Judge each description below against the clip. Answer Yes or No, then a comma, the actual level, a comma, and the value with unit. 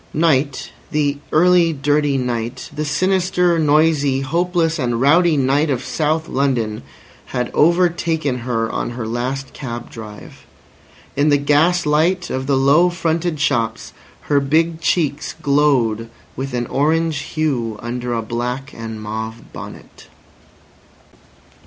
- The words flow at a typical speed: No, slow, 125 wpm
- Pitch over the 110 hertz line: Yes, medium, 140 Hz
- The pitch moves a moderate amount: Yes, average, 4.6 semitones